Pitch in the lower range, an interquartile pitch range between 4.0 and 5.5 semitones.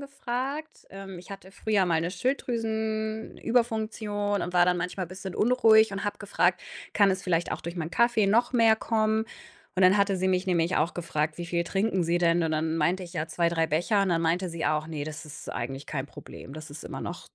No: medium, 185 Hz; average, 4.6 semitones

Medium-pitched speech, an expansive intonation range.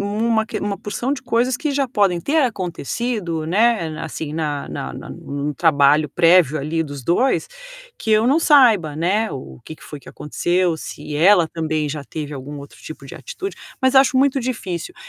Yes: medium, 175 Hz; wide, 7.5 semitones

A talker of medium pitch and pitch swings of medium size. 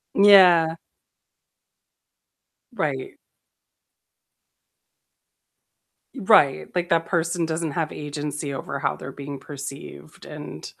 Yes: medium, 160 Hz; average, 3.5 semitones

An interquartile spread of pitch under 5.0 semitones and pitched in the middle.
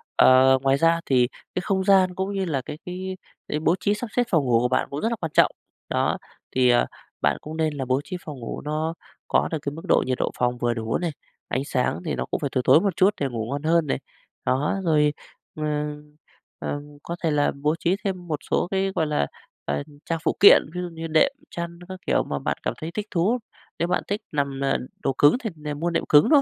Yes: average, 4.5 semitones; medium, 155 Hz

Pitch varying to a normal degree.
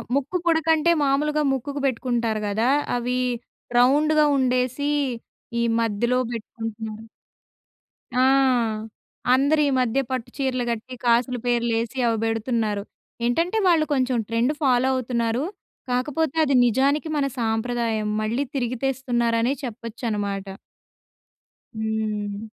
Yes: average, 3.2 semitones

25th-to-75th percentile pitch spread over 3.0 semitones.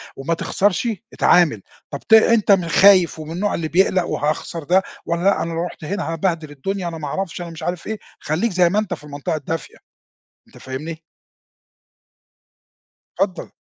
Yes: average, 3.4 semitones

